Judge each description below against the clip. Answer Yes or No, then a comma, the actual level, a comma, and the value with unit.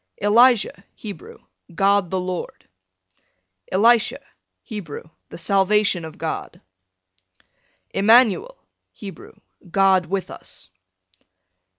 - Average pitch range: Yes, average, 3.0 semitones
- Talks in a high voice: Yes, high, 200 Hz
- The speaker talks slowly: Yes, slow, 80 wpm